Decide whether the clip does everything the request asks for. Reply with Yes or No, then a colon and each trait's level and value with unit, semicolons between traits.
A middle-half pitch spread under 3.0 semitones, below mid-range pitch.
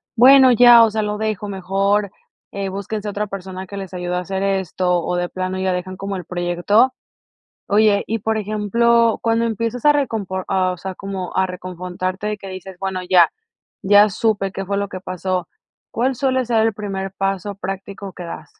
No: narrow, 2.5 semitones; high, 195 Hz